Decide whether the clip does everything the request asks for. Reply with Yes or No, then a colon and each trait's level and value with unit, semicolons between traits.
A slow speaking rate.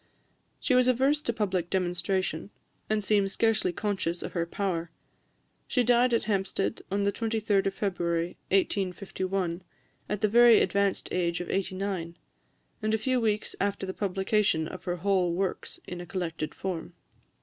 No: average, 160 wpm